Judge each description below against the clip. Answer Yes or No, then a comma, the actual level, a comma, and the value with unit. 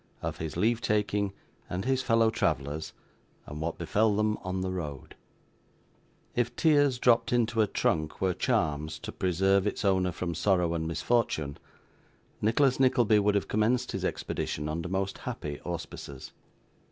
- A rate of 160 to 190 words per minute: No, average, 150 wpm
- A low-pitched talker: Yes, very low, 95 Hz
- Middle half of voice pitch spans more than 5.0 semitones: Yes, wide, 5.4 semitones